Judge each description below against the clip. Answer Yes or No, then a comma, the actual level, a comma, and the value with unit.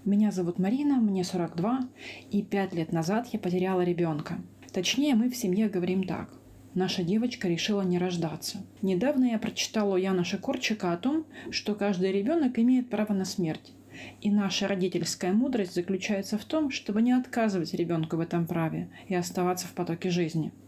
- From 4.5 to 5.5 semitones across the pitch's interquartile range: No, average, 3.6 semitones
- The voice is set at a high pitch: Yes, high, 195 Hz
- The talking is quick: Yes, fast, 165 wpm